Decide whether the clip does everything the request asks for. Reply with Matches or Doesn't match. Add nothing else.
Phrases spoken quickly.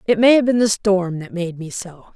Matches